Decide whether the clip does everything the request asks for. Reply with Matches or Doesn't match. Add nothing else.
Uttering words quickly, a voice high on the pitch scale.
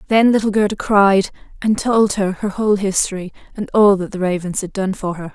Matches